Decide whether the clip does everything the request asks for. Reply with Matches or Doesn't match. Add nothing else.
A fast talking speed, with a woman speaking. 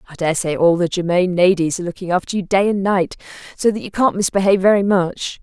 Matches